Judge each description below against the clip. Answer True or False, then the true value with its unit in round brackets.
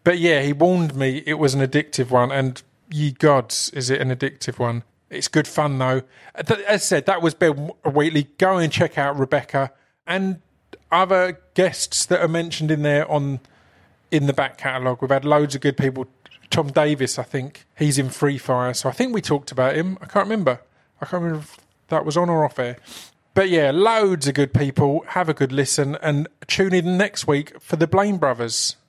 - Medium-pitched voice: True (150 Hz)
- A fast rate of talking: True (210 wpm)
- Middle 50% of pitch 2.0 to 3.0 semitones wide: False (4.0 semitones)